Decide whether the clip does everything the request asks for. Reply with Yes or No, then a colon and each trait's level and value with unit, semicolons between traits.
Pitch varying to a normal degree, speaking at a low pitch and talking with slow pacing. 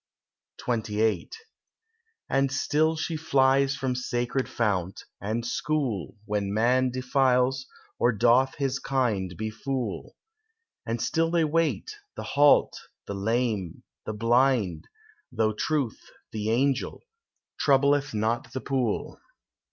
Yes: average, 3.9 semitones; low, 125 Hz; slow, 110 wpm